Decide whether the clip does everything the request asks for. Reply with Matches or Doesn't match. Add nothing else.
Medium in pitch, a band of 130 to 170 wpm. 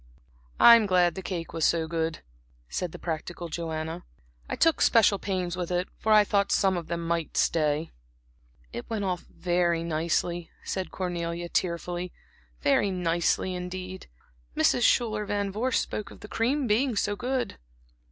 Matches